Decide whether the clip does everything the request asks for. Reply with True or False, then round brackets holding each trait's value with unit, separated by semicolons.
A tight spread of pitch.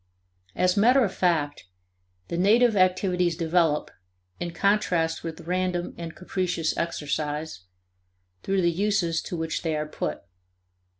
True (2.3 semitones)